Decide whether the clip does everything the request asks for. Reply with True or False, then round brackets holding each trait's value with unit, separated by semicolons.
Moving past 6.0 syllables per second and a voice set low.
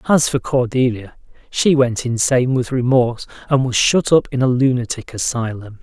False (5.1 syllables/s; 125 Hz)